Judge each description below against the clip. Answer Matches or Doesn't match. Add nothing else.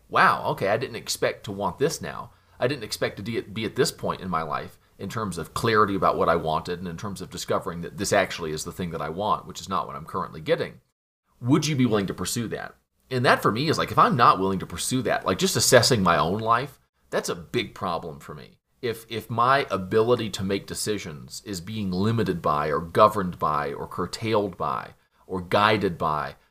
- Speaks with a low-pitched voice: Matches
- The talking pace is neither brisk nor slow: Doesn't match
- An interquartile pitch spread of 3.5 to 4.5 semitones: Matches